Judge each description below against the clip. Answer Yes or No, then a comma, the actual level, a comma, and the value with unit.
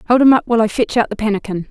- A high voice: Yes, high, 225 Hz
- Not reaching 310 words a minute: No, fast, 315 wpm